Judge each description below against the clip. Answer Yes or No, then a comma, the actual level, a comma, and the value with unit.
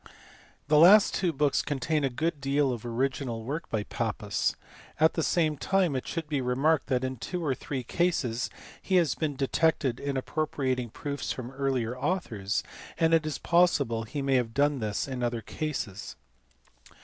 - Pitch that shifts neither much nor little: Yes, average, 3.9 semitones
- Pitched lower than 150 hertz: Yes, medium, 140 Hz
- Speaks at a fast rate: No, average, 175 wpm